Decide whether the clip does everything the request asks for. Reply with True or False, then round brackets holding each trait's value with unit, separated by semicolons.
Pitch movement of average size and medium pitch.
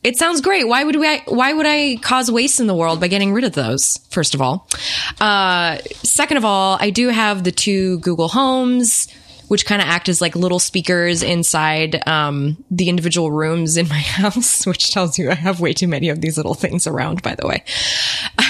False (5.7 semitones; 180 Hz)